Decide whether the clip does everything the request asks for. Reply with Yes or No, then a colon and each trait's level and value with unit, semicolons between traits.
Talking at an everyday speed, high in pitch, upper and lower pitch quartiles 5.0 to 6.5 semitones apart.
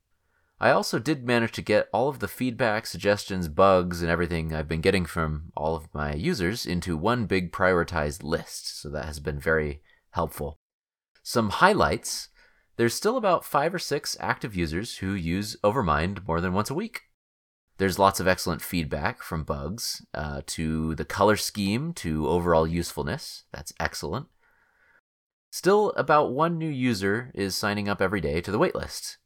No: average, 165 wpm; very low, 95 Hz; wide, 5.6 semitones